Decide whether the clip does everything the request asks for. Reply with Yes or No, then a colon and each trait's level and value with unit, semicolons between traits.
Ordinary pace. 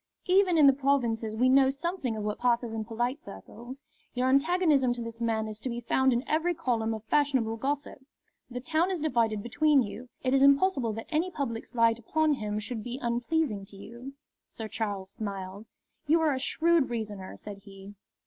Yes: average, 190 wpm